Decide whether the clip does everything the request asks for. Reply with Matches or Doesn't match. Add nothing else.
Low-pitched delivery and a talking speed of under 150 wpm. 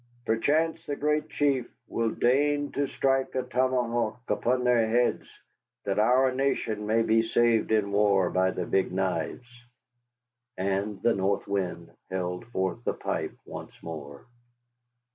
Matches